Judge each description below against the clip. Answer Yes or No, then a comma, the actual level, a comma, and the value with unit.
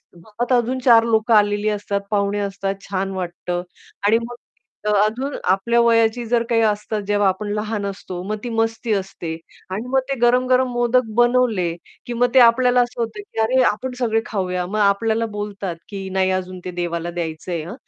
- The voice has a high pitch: Yes, high, 215 Hz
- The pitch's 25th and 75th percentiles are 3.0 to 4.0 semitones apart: Yes, average, 3.6 semitones